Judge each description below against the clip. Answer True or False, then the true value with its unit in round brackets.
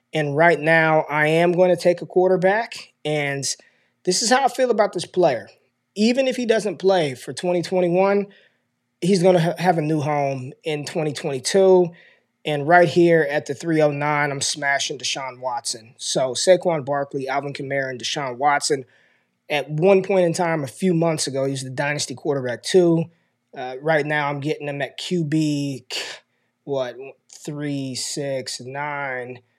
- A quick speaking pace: False (160 wpm)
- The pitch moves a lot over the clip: False (4.2 semitones)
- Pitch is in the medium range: True (155 Hz)